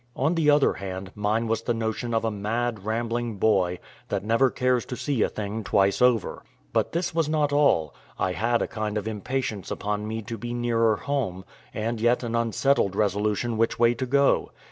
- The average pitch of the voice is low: Yes, low, 115 Hz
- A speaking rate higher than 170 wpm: Yes, average, 195 wpm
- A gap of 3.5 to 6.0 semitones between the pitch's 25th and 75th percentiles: No, average, 2.8 semitones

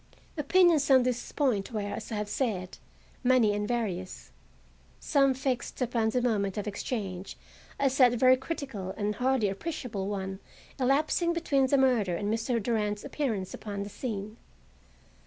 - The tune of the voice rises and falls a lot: No, average, 4.4 semitones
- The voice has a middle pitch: No, high, 230 Hz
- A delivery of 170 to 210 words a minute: No, average, 150 wpm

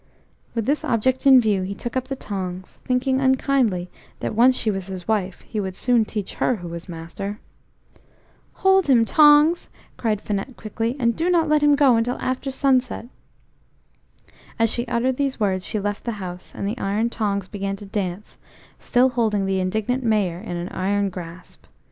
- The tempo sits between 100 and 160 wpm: No, average, 180 wpm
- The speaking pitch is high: Yes, high, 220 Hz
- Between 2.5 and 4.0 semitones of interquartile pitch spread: No, average, 4.8 semitones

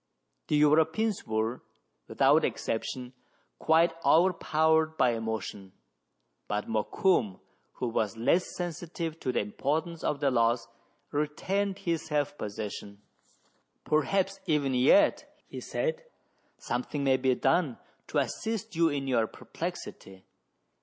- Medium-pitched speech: Yes, medium, 145 Hz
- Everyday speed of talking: No, slow, 125 wpm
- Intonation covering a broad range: Yes, wide, 6.3 semitones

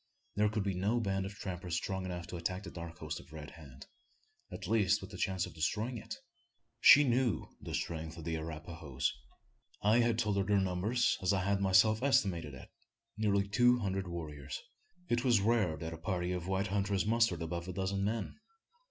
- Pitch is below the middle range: Yes, very low, 95 Hz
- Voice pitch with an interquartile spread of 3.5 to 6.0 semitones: Yes, average, 3.8 semitones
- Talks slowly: No, average, 195 wpm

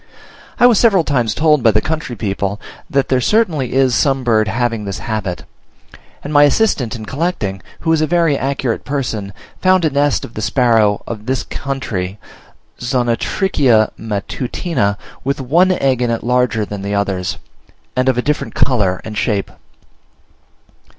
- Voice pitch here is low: Yes, low, 125 Hz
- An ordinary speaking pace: Yes, average, 160 wpm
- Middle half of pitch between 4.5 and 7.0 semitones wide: Yes, average, 5.2 semitones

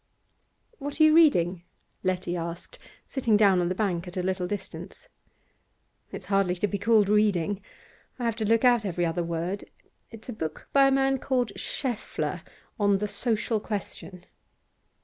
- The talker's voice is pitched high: Yes, high, 205 Hz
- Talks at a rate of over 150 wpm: Yes, average, 165 wpm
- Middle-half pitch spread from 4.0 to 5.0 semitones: Yes, average, 4.4 semitones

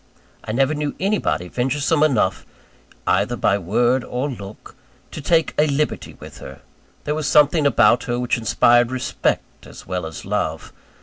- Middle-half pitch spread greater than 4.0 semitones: Yes, average, 5.1 semitones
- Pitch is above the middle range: No, low, 125 Hz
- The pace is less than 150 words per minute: No, average, 160 wpm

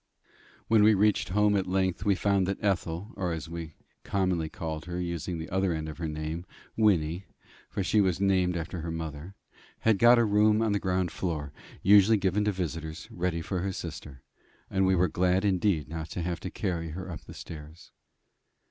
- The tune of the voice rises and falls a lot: No, average, 3.2 semitones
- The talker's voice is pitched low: Yes, very low, 90 Hz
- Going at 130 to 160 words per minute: No, average, 195 wpm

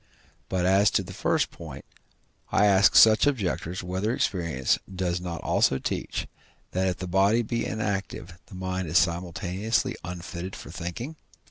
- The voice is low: Yes, very low, 95 Hz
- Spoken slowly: No, average, 150 wpm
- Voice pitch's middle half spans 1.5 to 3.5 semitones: Yes, average, 2.7 semitones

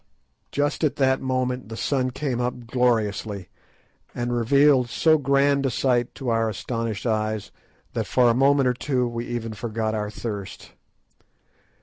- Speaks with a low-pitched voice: Yes, low, 120 Hz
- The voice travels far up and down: No, average, 2.8 semitones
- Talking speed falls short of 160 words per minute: Yes, average, 150 wpm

